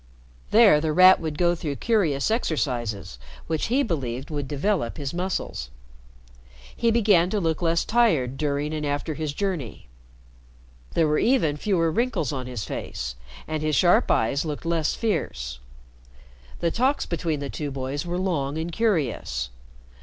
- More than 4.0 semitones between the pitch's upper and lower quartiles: Yes, average, 4.7 semitones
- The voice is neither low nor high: Yes, medium, 155 Hz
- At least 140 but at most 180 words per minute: Yes, average, 155 wpm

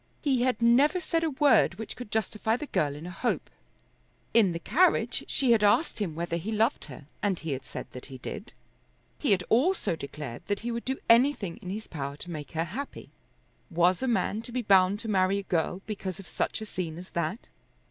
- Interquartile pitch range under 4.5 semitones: No, wide, 5.6 semitones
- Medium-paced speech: No, fast, 220 wpm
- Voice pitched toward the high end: Yes, high, 205 Hz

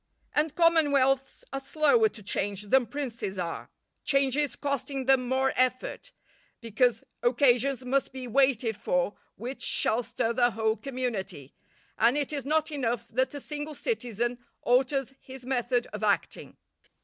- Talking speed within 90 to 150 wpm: Yes, average, 140 wpm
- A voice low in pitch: No, very high, 255 Hz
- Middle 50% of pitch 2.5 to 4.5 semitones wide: Yes, average, 3.1 semitones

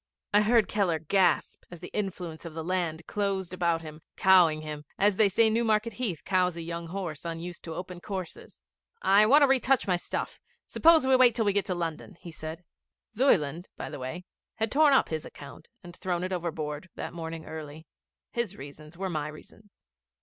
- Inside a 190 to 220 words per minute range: Yes, average, 195 wpm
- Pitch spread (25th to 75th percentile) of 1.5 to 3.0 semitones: No, average, 4.2 semitones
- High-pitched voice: No, medium, 180 Hz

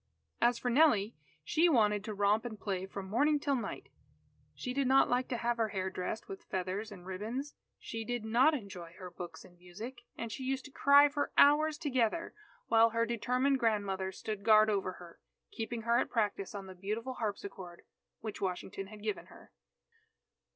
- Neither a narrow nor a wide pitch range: Yes, average, 4.4 semitones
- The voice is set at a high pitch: Yes, high, 220 Hz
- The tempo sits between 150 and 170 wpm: No, average, 185 wpm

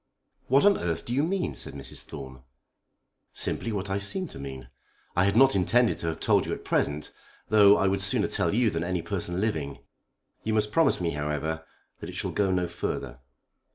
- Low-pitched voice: Yes, very low, 95 Hz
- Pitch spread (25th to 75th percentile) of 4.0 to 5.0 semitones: No, wide, 5.6 semitones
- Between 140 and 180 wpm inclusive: No, average, 200 wpm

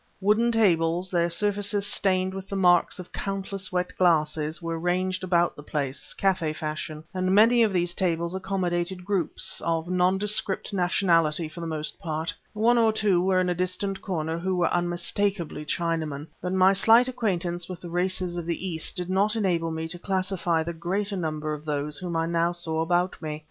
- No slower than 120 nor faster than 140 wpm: No, average, 185 wpm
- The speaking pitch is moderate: Yes, medium, 180 Hz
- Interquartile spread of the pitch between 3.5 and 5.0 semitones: No, narrow, 2.6 semitones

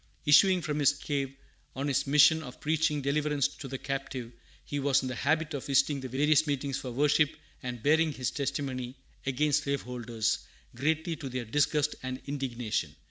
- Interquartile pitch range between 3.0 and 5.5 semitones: No, narrow, 2.6 semitones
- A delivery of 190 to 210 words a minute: No, average, 170 wpm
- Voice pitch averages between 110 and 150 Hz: Yes, medium, 140 Hz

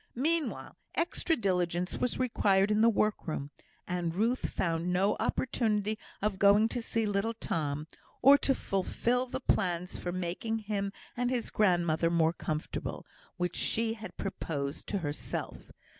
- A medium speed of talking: Yes, average, 145 wpm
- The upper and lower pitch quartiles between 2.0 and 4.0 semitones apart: No, average, 4.7 semitones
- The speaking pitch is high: Yes, high, 200 Hz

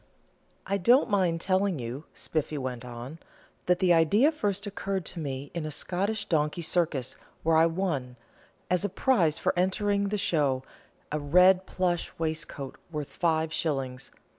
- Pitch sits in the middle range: Yes, medium, 165 Hz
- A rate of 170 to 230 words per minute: No, average, 155 wpm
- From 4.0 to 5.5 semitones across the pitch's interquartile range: Yes, average, 4.3 semitones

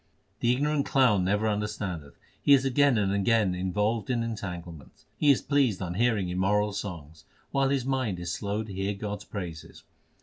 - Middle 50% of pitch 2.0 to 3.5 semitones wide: No, average, 4.8 semitones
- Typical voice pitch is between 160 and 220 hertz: No, low, 105 Hz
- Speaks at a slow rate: No, average, 175 wpm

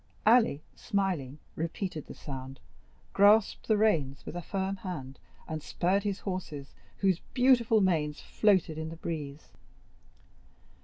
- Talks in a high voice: No, medium, 180 Hz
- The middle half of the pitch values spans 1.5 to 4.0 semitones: No, average, 5.2 semitones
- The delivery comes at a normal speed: No, slow, 125 wpm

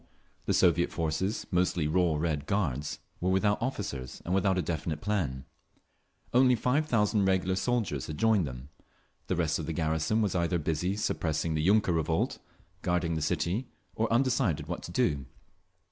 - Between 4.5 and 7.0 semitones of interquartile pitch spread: Yes, average, 4.9 semitones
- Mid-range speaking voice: No, very low, 90 Hz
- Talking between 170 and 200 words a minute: No, average, 160 wpm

